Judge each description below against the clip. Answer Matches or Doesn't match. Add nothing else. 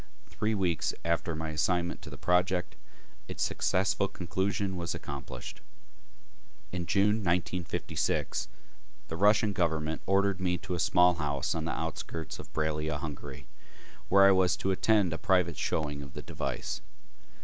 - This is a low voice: Matches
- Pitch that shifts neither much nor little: Matches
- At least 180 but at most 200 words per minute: Doesn't match